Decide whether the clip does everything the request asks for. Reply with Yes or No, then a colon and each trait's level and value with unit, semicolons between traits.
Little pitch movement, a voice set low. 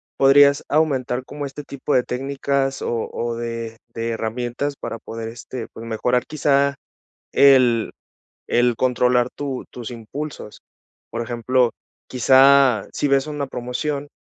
No: average, 3.0 semitones; low, 125 Hz